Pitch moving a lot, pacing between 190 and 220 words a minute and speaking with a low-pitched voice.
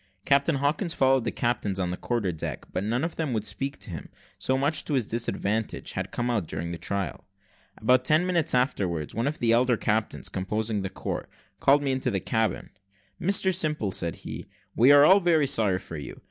Yes: wide, 6.1 semitones; fast, 205 wpm; low, 120 Hz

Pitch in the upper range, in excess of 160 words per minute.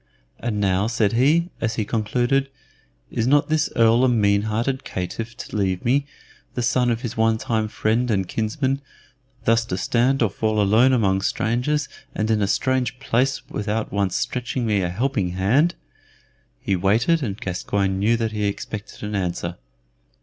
No: low, 115 Hz; average, 170 wpm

